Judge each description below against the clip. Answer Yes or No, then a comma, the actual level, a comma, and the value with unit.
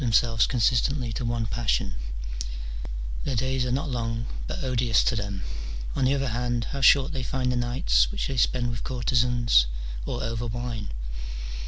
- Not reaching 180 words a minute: Yes, average, 170 wpm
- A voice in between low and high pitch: No, low, 120 Hz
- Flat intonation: Yes, narrow, 2.0 semitones